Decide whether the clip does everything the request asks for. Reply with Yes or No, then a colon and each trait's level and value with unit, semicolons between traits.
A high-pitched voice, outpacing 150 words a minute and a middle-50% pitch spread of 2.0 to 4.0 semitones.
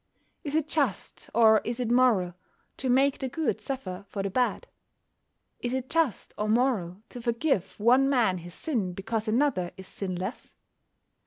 No: high, 235 Hz; average, 160 wpm; average, 5.2 semitones